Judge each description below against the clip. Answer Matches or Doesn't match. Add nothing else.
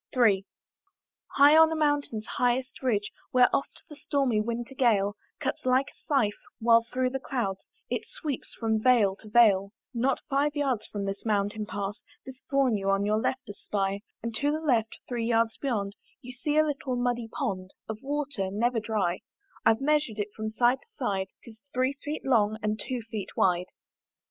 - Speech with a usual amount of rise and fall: Matches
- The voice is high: Matches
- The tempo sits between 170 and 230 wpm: Matches